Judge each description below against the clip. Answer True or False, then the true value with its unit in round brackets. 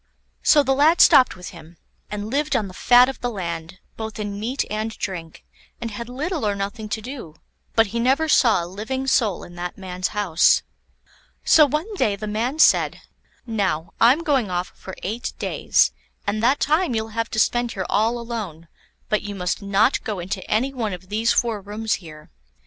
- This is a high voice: True (220 Hz)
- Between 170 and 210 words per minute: True (195 wpm)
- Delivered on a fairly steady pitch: False (4.4 semitones)